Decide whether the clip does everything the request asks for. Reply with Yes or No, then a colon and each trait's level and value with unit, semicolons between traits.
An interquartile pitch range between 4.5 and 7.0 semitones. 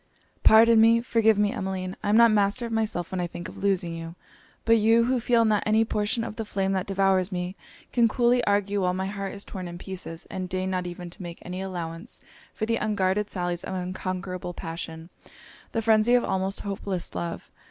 No: average, 3.4 semitones